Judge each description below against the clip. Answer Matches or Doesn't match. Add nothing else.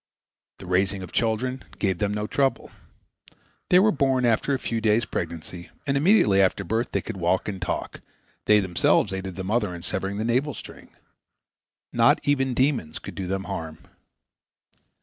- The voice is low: Matches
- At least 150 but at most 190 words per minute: Matches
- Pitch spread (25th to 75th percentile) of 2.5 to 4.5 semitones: Doesn't match